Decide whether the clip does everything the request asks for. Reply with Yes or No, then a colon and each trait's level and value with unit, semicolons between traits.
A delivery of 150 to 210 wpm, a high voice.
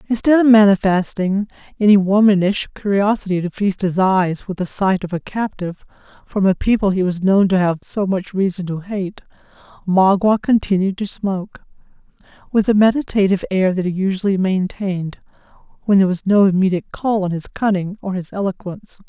Yes: average, 165 wpm; high, 195 Hz